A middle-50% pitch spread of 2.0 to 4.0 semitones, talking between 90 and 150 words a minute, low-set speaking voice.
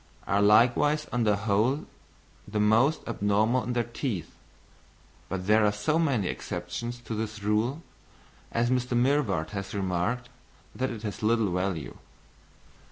Yes: average, 3.3 semitones; average, 140 wpm; low, 110 Hz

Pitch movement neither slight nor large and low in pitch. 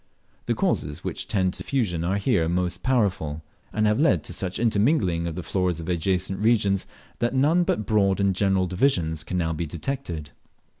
Yes: average, 4.0 semitones; very low, 95 Hz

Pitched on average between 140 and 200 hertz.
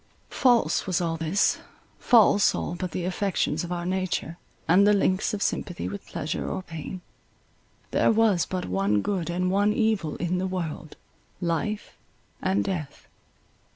Yes: medium, 185 Hz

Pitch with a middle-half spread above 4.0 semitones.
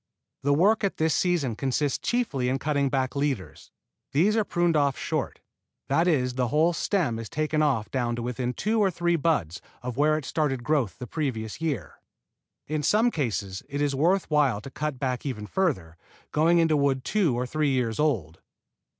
Yes: average, 4.4 semitones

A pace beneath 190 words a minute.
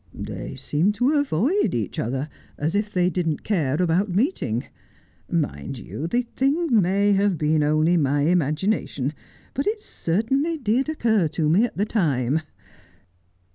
Yes: average, 150 wpm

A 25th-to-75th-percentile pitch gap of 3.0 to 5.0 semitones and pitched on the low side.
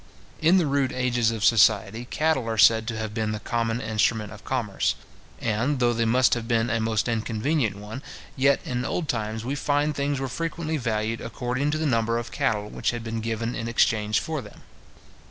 Yes: average, 3.3 semitones; low, 115 Hz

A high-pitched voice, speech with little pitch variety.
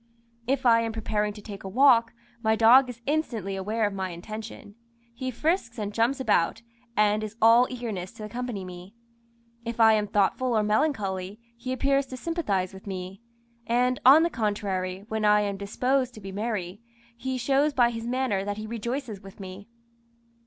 No: high, 220 Hz; average, 3.8 semitones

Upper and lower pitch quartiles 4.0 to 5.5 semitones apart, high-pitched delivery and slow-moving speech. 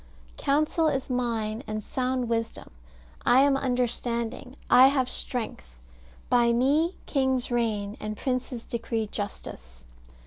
No: average, 2.8 semitones; high, 245 Hz; slow, 115 wpm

